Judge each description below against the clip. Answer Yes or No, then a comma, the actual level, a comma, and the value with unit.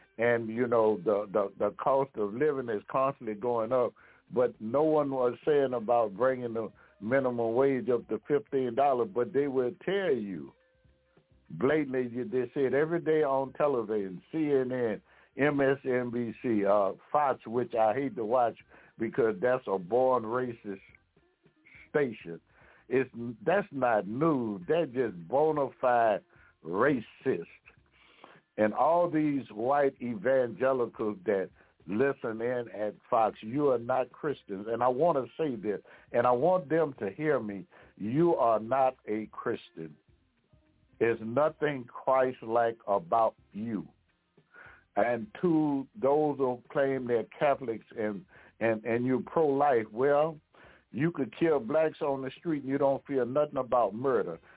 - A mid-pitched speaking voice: No, low, 125 Hz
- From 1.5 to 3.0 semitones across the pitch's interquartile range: No, average, 3.5 semitones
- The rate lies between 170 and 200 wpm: No, average, 140 wpm